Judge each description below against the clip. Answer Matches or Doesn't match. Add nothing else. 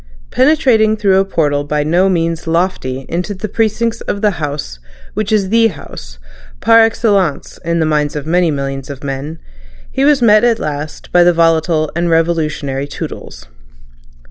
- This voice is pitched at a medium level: Matches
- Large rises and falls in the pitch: Matches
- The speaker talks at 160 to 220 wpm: Matches